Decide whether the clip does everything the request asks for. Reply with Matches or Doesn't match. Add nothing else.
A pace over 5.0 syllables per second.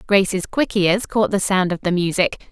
Doesn't match